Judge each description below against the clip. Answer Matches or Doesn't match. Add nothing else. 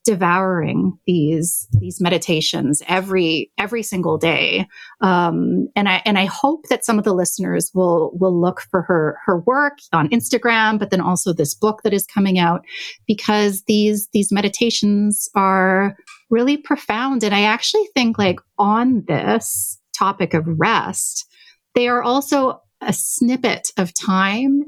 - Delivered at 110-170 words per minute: Matches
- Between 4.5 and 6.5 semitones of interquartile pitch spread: Matches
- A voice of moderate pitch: Doesn't match